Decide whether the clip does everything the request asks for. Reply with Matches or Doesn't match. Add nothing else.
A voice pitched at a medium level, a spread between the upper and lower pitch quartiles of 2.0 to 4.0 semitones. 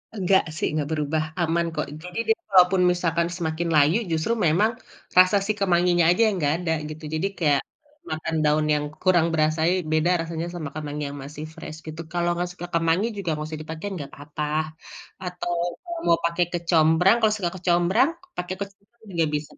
Matches